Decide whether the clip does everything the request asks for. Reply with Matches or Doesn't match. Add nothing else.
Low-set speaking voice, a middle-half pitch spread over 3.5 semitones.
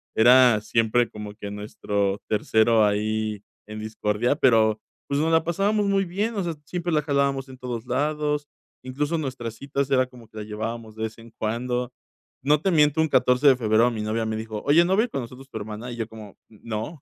Matches